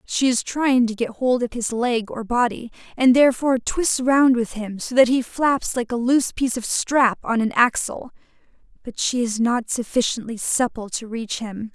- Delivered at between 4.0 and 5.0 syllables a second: Yes, 4.7 syllables/s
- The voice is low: No, high, 240 Hz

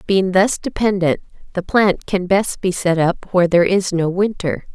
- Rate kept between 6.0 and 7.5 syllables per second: No, 4.7 syllables/s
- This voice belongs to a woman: Yes, female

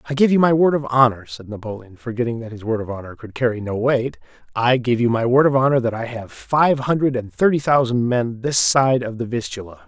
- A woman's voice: No, male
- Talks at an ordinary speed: No, fast, 235 wpm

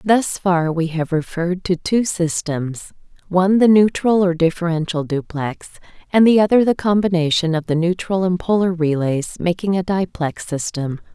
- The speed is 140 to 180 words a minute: Yes, average, 155 wpm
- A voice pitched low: No, medium, 175 Hz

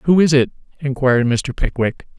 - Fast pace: No, average, 165 wpm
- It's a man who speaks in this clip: Yes, male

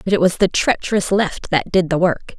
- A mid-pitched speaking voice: Yes, medium, 180 Hz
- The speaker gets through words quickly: Yes, fast, 250 wpm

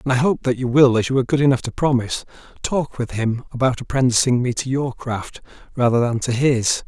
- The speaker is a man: Yes, male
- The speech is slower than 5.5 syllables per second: No, 5.7 syllables/s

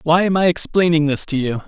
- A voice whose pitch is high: No, medium, 160 Hz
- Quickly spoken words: Yes, fast, 250 wpm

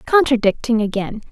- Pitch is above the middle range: Yes, high, 230 Hz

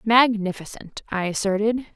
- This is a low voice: No, high, 210 Hz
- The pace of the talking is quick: No, slow, 90 wpm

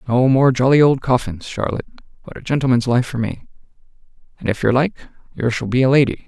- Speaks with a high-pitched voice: No, low, 125 Hz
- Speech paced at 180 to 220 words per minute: Yes, average, 200 wpm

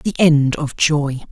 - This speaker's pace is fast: No, average, 180 wpm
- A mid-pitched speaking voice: Yes, medium, 150 Hz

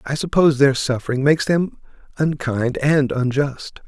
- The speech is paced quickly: No, average, 140 wpm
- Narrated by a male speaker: Yes, male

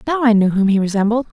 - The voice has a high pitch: Yes, high, 220 Hz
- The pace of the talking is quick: Yes, fast, 260 wpm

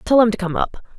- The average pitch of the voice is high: Yes, high, 215 Hz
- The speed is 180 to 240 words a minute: No, fast, 305 wpm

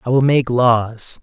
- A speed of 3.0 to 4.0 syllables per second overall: Yes, 3.6 syllables/s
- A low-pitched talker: Yes, low, 120 Hz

